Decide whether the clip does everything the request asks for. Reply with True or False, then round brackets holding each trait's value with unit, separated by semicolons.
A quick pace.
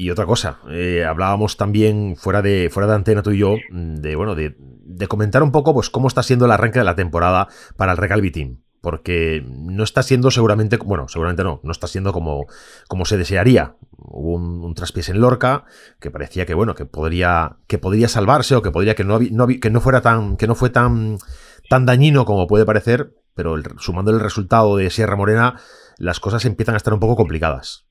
True (210 wpm)